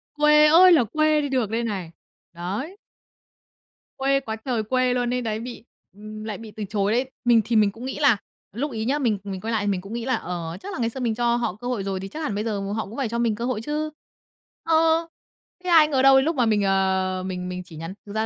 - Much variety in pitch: No, average, 4.6 semitones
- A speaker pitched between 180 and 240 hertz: Yes, high, 230 Hz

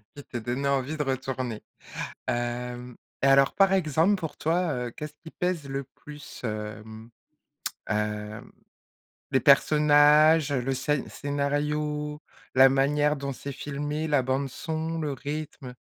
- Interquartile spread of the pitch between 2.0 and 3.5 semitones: Yes, average, 2.9 semitones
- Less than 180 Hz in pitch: Yes, medium, 140 Hz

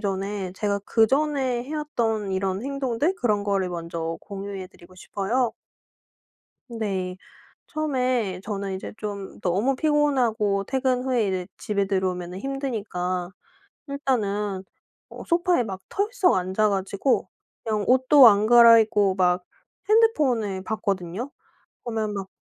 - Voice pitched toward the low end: No, high, 210 Hz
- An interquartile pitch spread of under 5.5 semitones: Yes, average, 5.1 semitones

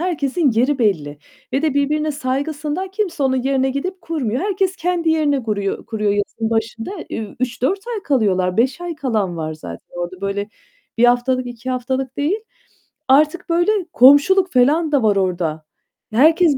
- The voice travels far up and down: Yes, wide, 6.1 semitones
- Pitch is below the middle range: No, very high, 265 Hz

